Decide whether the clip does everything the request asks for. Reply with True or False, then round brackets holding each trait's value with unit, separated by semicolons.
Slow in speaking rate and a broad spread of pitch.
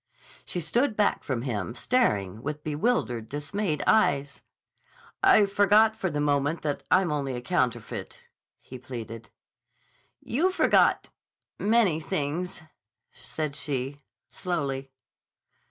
True (105 wpm; 6.7 semitones)